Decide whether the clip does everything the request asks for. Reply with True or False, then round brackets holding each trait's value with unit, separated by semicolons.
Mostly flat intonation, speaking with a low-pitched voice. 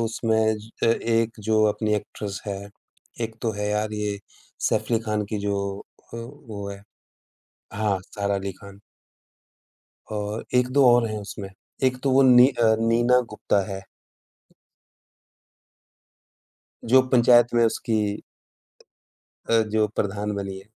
True (2.3 semitones; 110 Hz)